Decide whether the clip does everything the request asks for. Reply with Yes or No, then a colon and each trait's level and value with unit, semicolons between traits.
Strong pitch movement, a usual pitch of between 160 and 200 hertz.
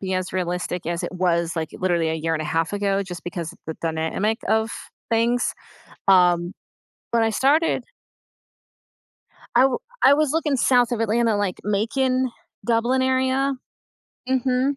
No: wide, 6.5 semitones; high, 210 Hz